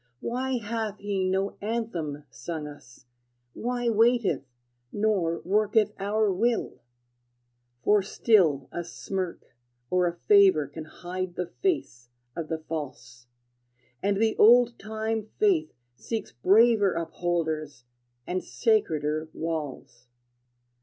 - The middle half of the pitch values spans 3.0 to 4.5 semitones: No, wide, 5.5 semitones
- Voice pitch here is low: No, high, 190 Hz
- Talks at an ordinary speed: No, slow, 110 wpm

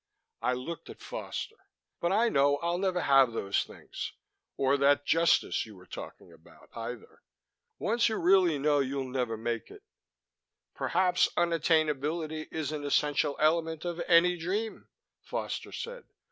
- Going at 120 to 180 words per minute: Yes, average, 145 wpm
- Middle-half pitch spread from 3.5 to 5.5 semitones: Yes, average, 4.2 semitones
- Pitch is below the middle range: No, medium, 155 Hz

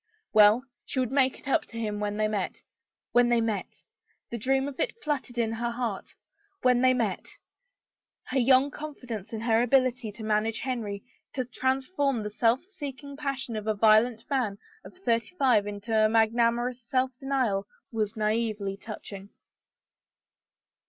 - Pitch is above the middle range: Yes, high, 235 Hz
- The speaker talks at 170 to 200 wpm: No, average, 155 wpm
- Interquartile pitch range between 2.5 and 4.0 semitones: Yes, average, 3.3 semitones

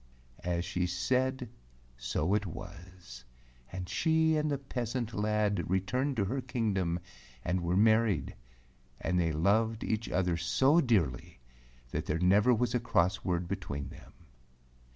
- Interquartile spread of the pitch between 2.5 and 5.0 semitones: No, wide, 5.4 semitones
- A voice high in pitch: No, low, 100 Hz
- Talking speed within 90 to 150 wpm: Yes, average, 140 wpm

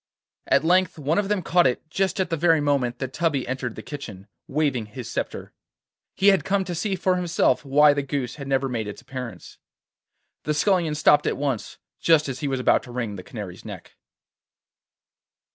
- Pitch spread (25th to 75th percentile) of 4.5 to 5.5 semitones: Yes, average, 5.1 semitones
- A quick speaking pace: No, average, 195 wpm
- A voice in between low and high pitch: Yes, medium, 145 Hz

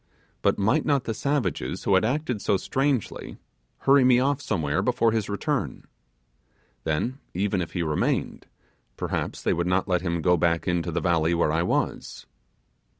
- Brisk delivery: No, average, 165 wpm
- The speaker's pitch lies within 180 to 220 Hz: No, very low, 95 Hz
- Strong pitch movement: Yes, wide, 6.7 semitones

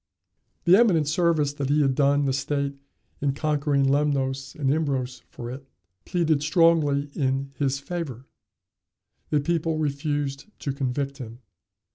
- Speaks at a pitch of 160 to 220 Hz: No, medium, 140 Hz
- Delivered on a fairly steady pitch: Yes, narrow, 2.0 semitones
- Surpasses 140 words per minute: No, slow, 135 wpm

